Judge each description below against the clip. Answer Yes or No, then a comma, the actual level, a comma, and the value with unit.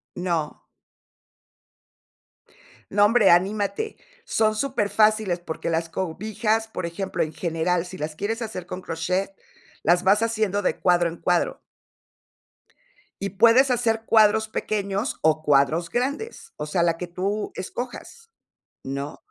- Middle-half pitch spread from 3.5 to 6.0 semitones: Yes, average, 4.2 semitones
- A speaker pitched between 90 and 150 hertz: No, high, 195 Hz